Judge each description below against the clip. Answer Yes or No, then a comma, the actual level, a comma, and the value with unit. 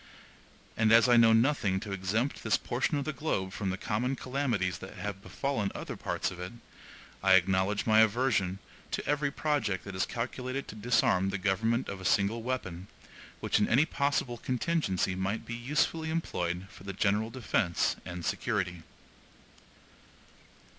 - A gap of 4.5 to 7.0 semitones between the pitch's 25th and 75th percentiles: Yes, average, 5.1 semitones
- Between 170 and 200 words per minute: No, average, 160 wpm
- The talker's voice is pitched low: Yes, low, 110 Hz